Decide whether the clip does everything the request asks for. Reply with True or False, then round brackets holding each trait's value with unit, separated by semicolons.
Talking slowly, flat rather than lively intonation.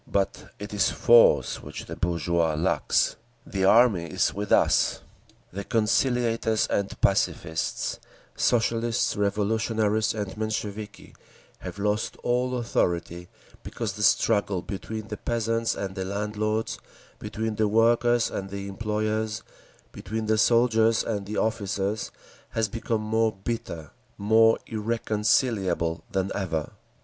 True (120 wpm; 2.3 semitones)